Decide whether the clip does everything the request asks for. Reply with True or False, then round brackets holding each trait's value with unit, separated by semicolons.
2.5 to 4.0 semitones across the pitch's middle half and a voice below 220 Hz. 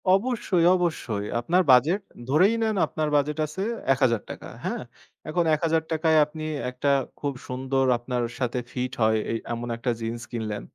False (5.3 semitones; 140 Hz)